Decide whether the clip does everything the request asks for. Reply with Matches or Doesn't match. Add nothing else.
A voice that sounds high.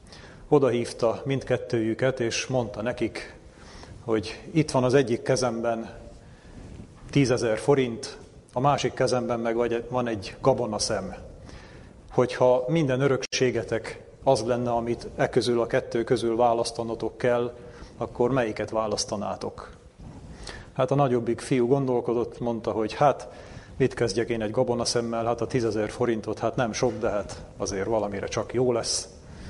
Doesn't match